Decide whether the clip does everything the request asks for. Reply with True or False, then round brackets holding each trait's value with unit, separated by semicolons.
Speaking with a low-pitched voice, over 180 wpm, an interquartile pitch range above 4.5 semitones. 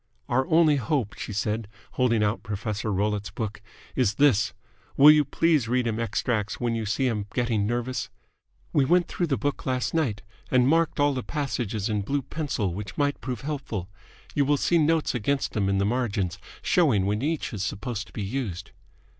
True (120 Hz; 190 wpm; 5.2 semitones)